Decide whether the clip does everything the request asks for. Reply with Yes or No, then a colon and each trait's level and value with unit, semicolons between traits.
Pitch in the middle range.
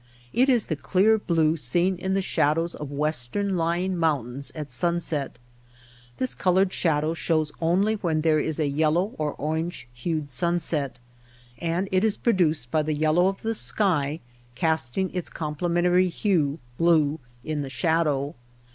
Yes: medium, 160 Hz